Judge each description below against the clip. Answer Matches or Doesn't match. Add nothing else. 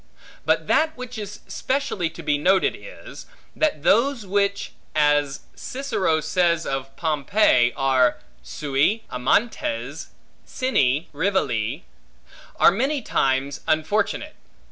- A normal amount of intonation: Doesn't match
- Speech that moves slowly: Matches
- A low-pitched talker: Doesn't match